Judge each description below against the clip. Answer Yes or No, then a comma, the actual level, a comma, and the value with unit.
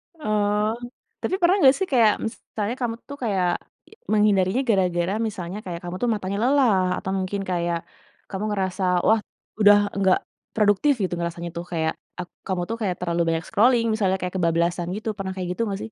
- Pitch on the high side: Yes, high, 195 Hz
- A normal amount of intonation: Yes, average, 3.4 semitones